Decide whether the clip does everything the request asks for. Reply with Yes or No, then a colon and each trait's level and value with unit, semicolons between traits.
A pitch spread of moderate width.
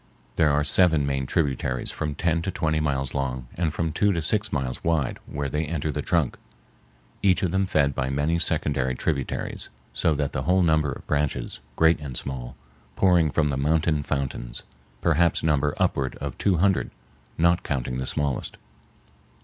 Yes: average, 3.5 semitones